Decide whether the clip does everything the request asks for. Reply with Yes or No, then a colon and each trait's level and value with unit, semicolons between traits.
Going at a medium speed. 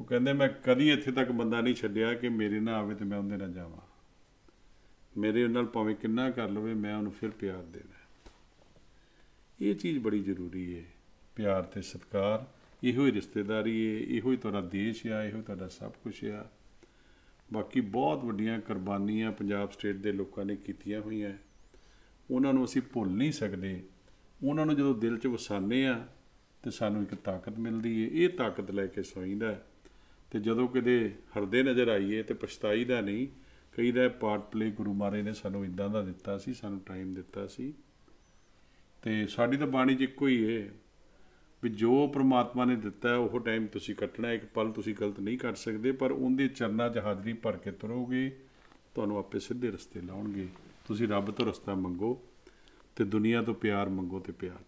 Yes: average, 175 wpm